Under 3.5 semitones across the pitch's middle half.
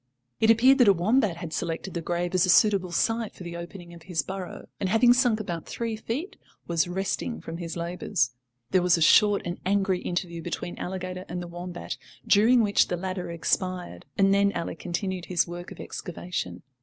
Yes: average, 2.8 semitones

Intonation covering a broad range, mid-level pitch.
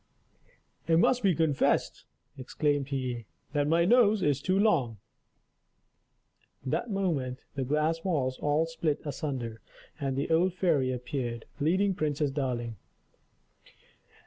No: average, 4.3 semitones; medium, 145 Hz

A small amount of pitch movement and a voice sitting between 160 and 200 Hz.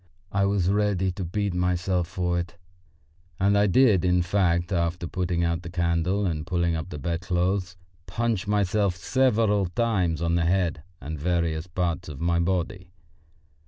No: narrow, 2.3 semitones; very low, 90 Hz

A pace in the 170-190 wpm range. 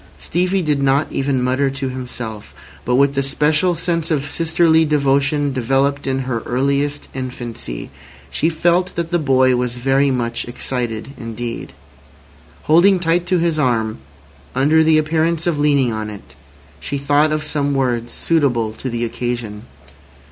No: average, 150 wpm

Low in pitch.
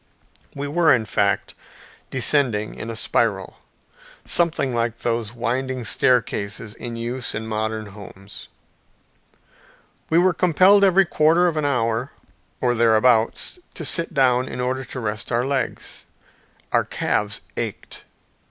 Yes: low, 125 Hz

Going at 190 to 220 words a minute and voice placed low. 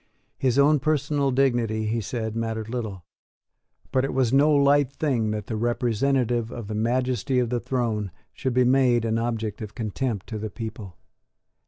No: average, 170 wpm; low, 120 Hz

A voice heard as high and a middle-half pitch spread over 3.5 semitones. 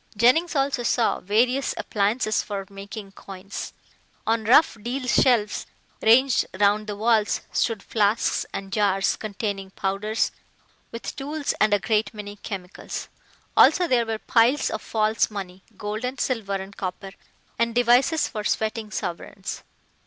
No: high, 215 Hz; average, 3.1 semitones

